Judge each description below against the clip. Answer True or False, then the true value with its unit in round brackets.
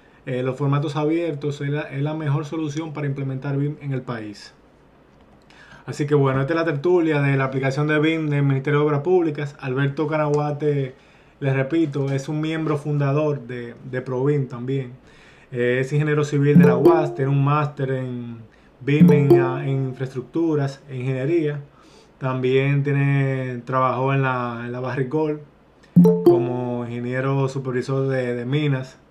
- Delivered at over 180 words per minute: False (155 wpm)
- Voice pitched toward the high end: False (140 Hz)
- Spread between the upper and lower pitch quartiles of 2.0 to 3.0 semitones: True (2.4 semitones)